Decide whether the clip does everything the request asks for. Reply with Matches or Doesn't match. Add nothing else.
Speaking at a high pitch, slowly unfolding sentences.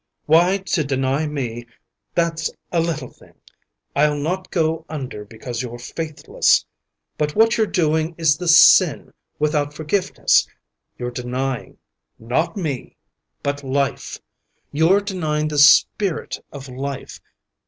Doesn't match